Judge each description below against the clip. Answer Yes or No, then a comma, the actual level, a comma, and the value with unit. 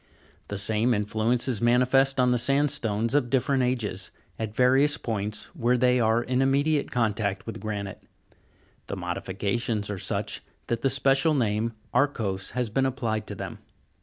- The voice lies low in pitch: Yes, low, 120 Hz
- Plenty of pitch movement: No, average, 3.8 semitones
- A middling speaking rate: Yes, average, 155 wpm